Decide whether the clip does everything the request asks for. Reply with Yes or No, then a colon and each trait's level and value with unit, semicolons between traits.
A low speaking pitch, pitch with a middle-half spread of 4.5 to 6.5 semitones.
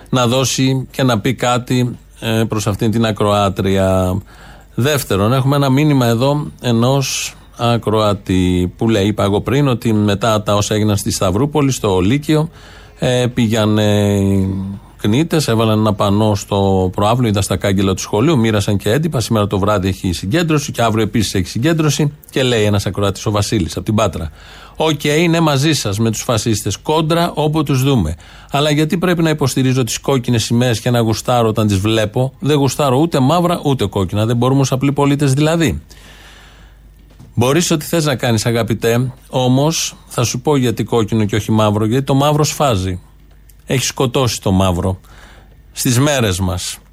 Yes: low, 115 Hz; average, 5.0 semitones